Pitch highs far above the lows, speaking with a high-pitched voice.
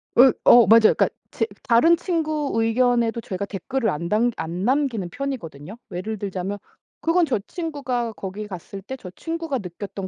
Yes: wide, 5.7 semitones; high, 225 Hz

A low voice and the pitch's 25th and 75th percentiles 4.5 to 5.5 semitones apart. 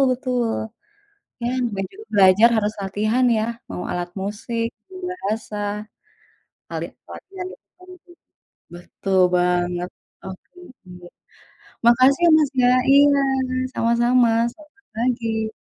No: high, 230 Hz; average, 4.9 semitones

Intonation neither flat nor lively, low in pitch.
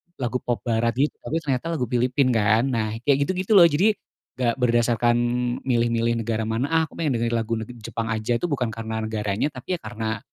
Yes: average, 3.5 semitones; low, 120 Hz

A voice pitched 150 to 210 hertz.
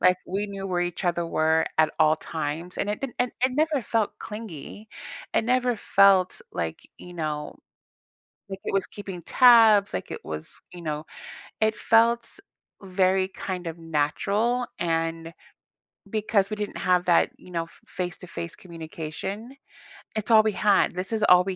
Yes: medium, 185 Hz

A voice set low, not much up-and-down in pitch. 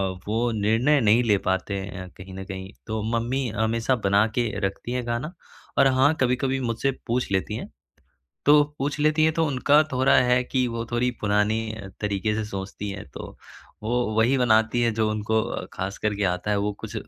No: low, 115 Hz; average, 3.5 semitones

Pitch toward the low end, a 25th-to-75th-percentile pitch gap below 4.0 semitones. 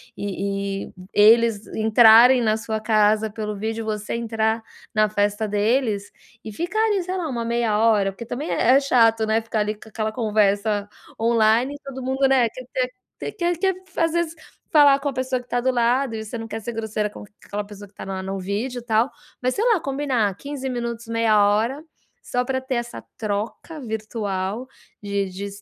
No: high, 225 Hz; average, 3.4 semitones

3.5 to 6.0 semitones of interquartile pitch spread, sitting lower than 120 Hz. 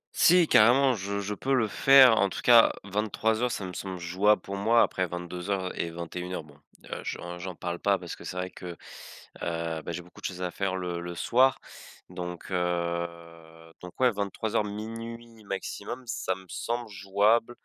Yes: average, 4.2 semitones; very low, 95 Hz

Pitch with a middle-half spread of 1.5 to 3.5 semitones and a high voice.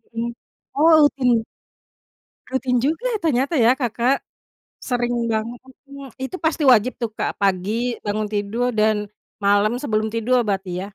Yes: average, 3.1 semitones; high, 235 Hz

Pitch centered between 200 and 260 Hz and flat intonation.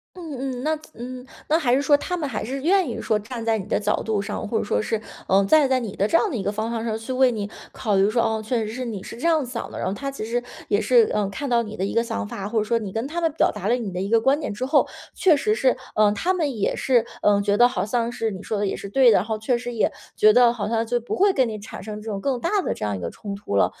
No: high, 230 Hz; average, 4.1 semitones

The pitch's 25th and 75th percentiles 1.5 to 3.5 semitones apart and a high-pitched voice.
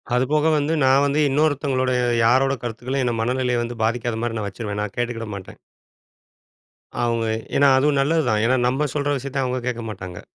No: average, 3.2 semitones; low, 125 Hz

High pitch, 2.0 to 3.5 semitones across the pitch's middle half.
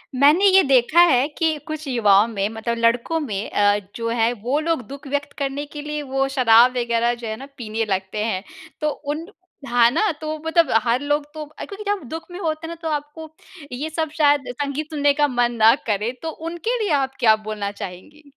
No: very high, 275 Hz; average, 5.0 semitones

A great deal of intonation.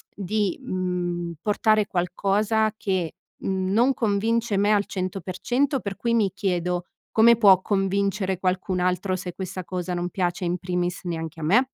No: average, 2.7 semitones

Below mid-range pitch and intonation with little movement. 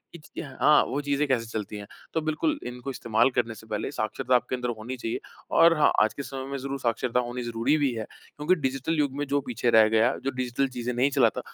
No: low, 125 Hz; average, 3.2 semitones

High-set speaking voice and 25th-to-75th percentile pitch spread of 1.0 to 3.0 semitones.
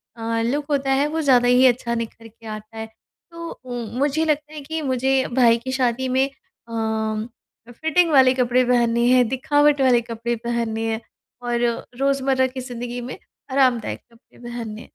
Yes: high, 245 Hz; narrow, 2.6 semitones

